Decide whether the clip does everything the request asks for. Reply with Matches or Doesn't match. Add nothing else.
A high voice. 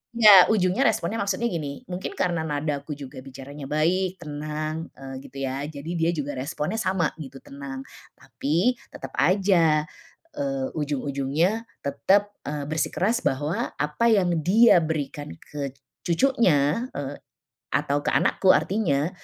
Doesn't match